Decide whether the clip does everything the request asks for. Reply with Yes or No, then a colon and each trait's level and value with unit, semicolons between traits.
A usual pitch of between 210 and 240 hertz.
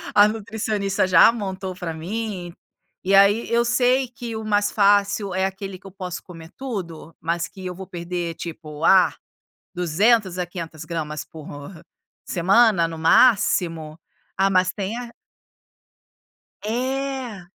No: high, 190 Hz